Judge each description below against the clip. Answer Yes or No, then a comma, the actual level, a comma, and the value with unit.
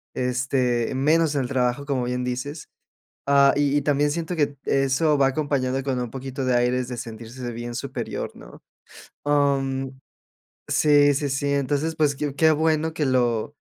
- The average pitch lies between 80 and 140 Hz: Yes, low, 135 Hz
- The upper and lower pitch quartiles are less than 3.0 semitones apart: Yes, narrow, 2.5 semitones